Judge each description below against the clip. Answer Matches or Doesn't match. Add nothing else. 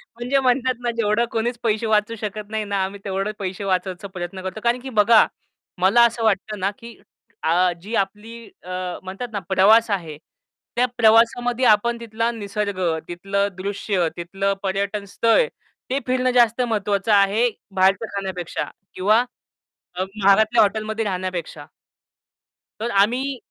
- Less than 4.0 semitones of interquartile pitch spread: Matches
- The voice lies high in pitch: Matches